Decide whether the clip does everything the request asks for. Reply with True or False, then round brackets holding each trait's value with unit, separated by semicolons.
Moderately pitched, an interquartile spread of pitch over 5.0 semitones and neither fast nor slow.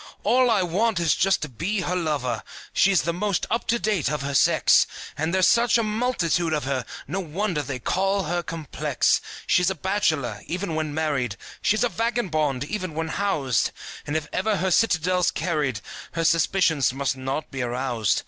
True (165 Hz; 5.4 semitones; 180 wpm)